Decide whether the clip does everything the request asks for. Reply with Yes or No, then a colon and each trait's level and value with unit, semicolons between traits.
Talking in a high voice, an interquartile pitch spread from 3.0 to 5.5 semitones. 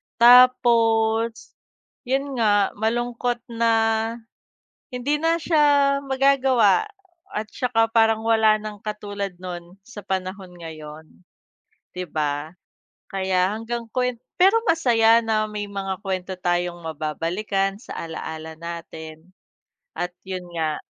Yes: high, 215 Hz; average, 5.1 semitones